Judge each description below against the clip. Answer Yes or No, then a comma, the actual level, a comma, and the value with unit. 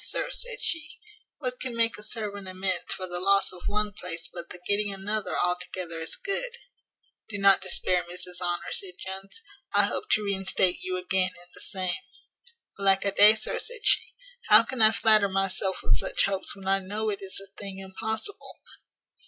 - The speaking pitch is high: Yes, high, 195 Hz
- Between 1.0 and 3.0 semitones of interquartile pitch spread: Yes, narrow, 2.6 semitones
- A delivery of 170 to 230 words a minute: Yes, average, 185 wpm